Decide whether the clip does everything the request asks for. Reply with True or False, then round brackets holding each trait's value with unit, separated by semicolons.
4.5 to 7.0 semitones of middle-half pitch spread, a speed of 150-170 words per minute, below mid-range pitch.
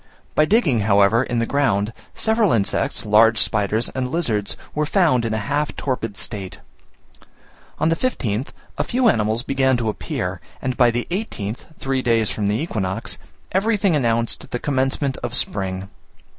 True (5.4 semitones; 155 wpm; 120 Hz)